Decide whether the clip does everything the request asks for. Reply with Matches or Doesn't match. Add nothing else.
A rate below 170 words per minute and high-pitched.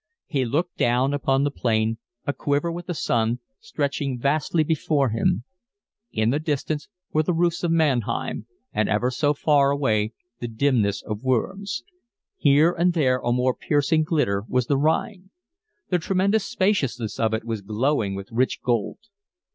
Doesn't match